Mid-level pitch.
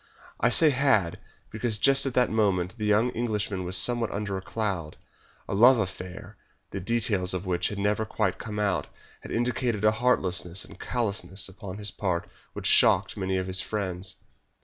No: low, 105 Hz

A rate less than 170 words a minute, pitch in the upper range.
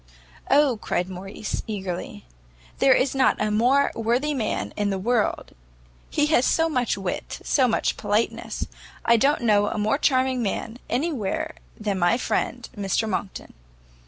Yes: average, 150 wpm; high, 230 Hz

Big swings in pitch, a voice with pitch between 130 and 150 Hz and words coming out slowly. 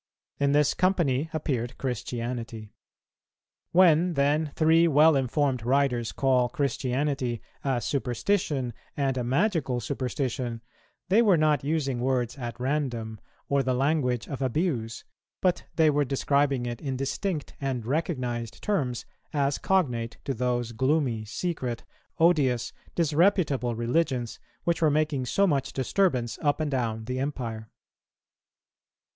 No: average, 3.9 semitones; low, 135 Hz; slow, 125 wpm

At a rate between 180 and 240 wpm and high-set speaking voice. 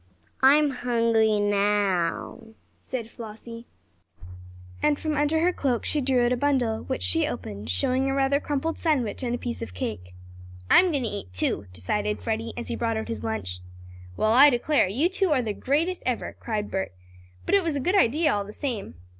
Yes: average, 190 wpm; high, 240 Hz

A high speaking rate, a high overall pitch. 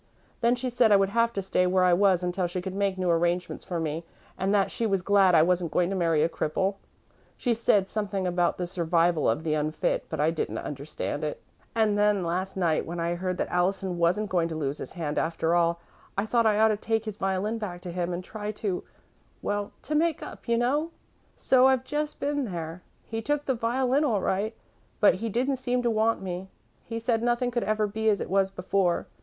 Yes: fast, 225 wpm; high, 195 Hz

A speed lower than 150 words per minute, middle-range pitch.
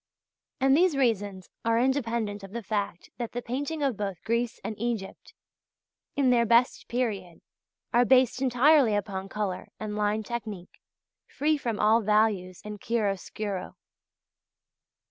No: slow, 135 wpm; high, 225 Hz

